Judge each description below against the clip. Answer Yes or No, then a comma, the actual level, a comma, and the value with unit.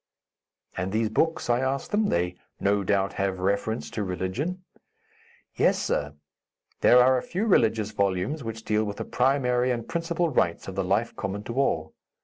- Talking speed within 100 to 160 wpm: No, average, 170 wpm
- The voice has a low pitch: Yes, low, 110 Hz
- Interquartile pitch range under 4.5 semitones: No, average, 5.2 semitones